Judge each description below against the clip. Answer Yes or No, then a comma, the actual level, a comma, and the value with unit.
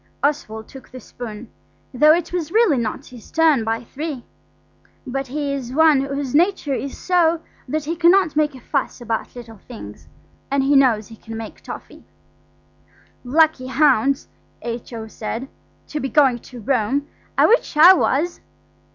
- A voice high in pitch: Yes, very high, 275 Hz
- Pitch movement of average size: Yes, average, 4.4 semitones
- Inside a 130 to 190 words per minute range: Yes, average, 155 wpm